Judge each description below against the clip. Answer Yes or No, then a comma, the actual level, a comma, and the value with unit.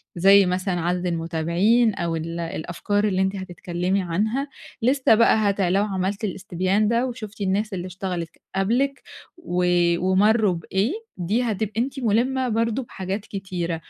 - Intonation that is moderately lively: Yes, average, 3.6 semitones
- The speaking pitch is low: No, high, 195 Hz